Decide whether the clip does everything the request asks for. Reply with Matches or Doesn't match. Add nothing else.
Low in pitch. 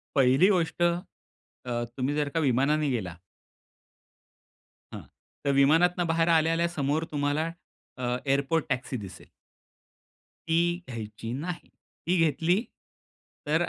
Doesn't match